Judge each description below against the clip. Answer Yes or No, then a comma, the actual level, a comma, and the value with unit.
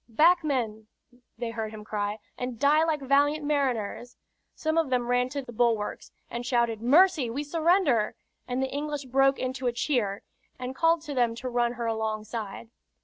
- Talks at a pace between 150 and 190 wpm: Yes, average, 175 wpm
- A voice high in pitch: Yes, very high, 250 Hz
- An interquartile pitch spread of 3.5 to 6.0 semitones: Yes, average, 4.0 semitones